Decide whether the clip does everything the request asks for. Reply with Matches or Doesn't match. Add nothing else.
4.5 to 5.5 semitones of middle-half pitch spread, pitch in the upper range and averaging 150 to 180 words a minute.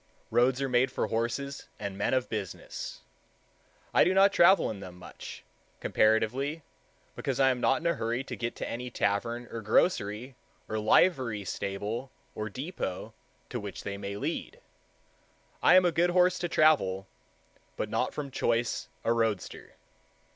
Doesn't match